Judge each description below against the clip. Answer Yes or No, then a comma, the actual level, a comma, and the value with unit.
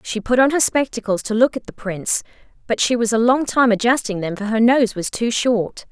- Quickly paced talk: Yes, fast, 245 wpm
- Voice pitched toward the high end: Yes, high, 230 Hz